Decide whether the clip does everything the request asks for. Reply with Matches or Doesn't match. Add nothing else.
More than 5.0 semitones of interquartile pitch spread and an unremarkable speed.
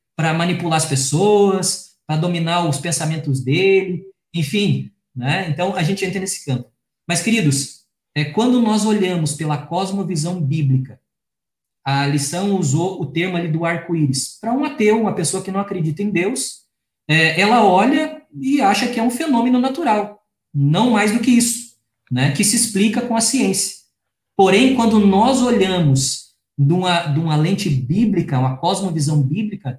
Matches